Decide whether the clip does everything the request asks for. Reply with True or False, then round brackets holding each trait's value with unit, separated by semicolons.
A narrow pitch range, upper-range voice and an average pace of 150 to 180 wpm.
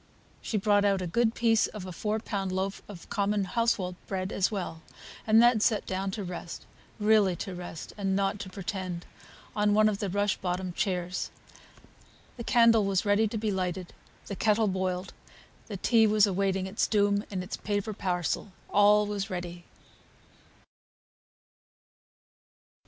True (2.2 semitones; 200 Hz; 155 wpm)